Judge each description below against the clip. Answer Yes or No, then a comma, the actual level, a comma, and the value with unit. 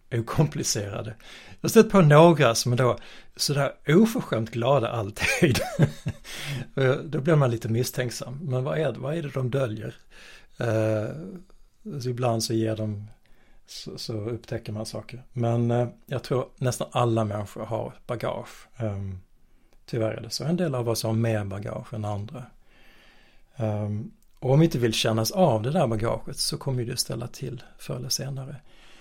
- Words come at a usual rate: Yes, average, 165 wpm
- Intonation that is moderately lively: Yes, average, 3.7 semitones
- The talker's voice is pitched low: Yes, low, 120 Hz